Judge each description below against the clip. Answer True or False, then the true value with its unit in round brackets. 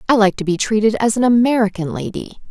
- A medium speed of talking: False (215 wpm)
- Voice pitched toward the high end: True (210 Hz)